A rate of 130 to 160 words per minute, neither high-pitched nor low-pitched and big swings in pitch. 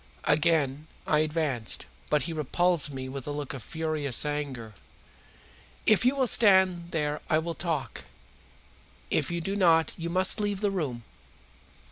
No: average, 150 wpm; medium, 160 Hz; average, 3.4 semitones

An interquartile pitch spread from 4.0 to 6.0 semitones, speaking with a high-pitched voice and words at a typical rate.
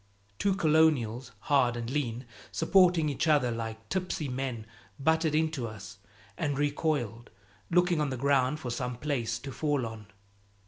No: average, 4.7 semitones; low, 135 Hz; average, 145 wpm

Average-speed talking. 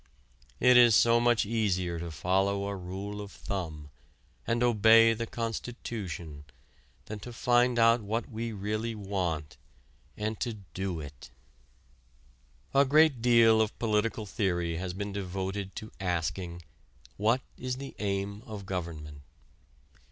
No: slow, 130 wpm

